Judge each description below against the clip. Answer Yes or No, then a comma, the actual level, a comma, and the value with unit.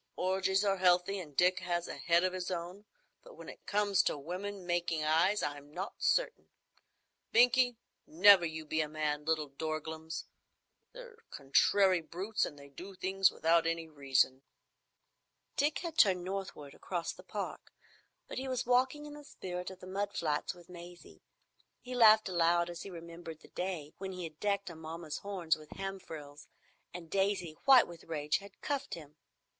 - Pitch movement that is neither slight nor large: Yes, average, 3.8 semitones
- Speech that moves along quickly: No, average, 175 wpm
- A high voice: No, medium, 180 Hz